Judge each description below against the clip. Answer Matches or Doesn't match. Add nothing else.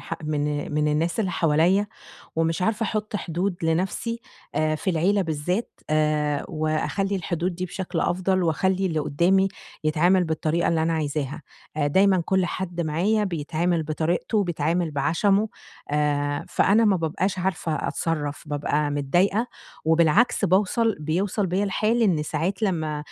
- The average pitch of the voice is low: Doesn't match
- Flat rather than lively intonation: Doesn't match